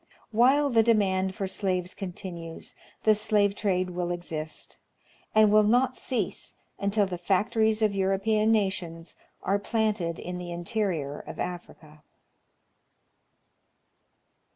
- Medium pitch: No, high, 195 Hz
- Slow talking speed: Yes, slow, 115 wpm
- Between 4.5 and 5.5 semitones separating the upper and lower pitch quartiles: No, average, 3.5 semitones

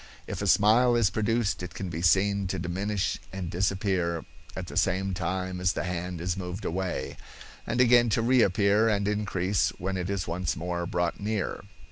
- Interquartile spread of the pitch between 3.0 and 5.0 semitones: No, narrow, 2.6 semitones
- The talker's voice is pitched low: Yes, very low, 95 Hz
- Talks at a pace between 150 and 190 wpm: Yes, average, 180 wpm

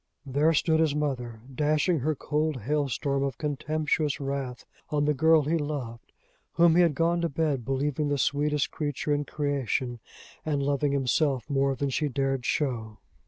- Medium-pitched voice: Yes, medium, 145 Hz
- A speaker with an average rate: Yes, average, 165 wpm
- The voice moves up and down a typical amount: No, narrow, 2.2 semitones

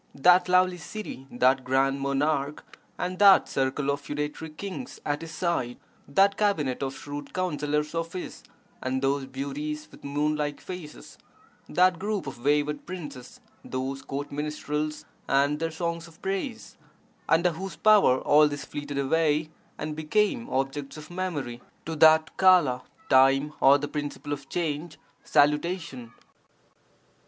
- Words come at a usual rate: Yes, average, 145 wpm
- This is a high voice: No, medium, 150 Hz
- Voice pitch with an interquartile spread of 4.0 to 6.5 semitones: No, average, 3.5 semitones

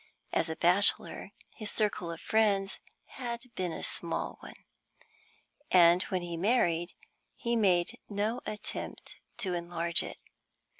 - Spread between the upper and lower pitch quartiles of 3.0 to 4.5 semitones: Yes, average, 3.9 semitones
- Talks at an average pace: No, slow, 130 wpm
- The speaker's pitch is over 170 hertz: Yes, medium, 185 Hz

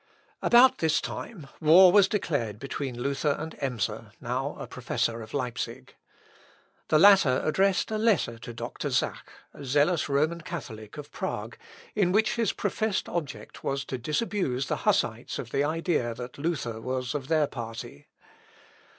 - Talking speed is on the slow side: No, average, 150 wpm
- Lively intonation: Yes, wide, 6.2 semitones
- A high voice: No, medium, 145 Hz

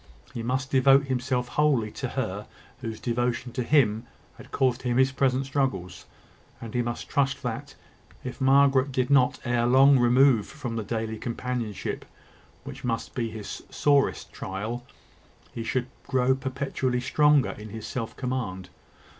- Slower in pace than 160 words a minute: Yes, average, 150 wpm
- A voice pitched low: Yes, low, 125 Hz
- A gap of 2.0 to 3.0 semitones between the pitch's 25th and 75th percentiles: Yes, narrow, 2.6 semitones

